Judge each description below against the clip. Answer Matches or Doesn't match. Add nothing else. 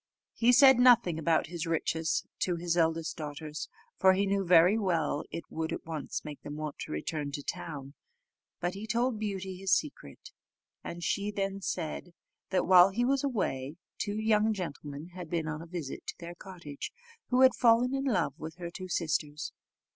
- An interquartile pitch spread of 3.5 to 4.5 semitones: Matches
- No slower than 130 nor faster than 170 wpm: Doesn't match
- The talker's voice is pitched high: Doesn't match